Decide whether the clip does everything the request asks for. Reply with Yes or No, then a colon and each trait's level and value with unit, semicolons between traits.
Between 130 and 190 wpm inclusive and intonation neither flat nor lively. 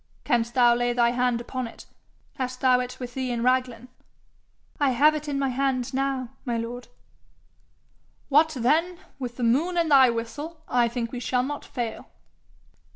No: average, 170 wpm; narrow, 2.3 semitones